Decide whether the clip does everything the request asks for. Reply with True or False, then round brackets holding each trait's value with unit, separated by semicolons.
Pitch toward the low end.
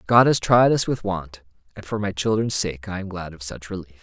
True (100 Hz)